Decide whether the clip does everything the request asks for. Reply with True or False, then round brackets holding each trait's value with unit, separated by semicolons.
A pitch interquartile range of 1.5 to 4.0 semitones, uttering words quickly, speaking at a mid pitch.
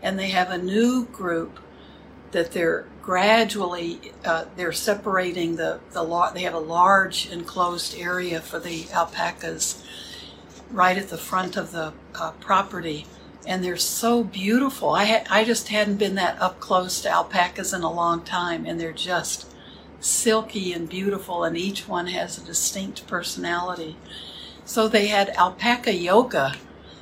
False (2.8 semitones; 155 wpm; 180 Hz)